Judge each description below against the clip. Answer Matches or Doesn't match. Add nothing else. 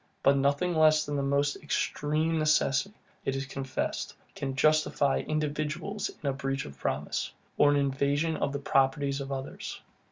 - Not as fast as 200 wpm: Matches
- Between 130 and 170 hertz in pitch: Matches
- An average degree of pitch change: Doesn't match